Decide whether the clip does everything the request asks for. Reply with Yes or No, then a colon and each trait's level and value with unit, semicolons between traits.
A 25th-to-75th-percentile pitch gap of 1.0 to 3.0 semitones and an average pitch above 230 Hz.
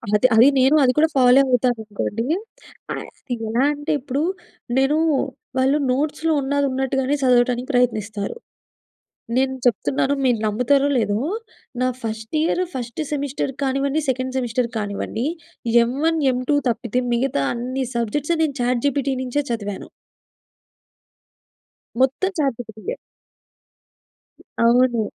Yes: average, 2.7 semitones; very high, 255 Hz